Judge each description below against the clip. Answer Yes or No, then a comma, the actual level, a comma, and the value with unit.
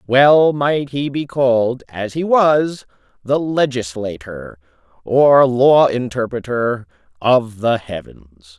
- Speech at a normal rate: No, slow, 110 wpm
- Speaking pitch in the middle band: No, low, 125 Hz